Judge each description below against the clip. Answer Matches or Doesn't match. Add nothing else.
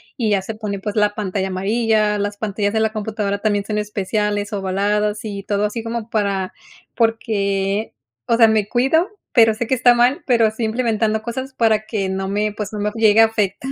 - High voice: Matches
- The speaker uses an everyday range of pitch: Doesn't match